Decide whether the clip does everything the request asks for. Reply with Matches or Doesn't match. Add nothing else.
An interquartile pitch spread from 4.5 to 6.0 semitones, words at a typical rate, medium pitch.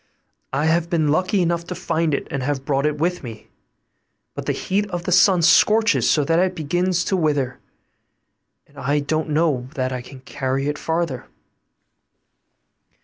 Doesn't match